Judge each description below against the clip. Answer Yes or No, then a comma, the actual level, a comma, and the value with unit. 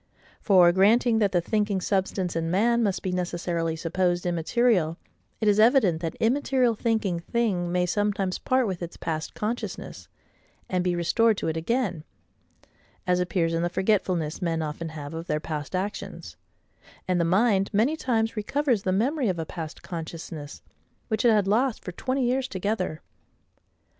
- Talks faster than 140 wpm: Yes, average, 165 wpm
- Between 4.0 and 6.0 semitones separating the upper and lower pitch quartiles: Yes, average, 4.7 semitones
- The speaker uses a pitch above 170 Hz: Yes, medium, 185 Hz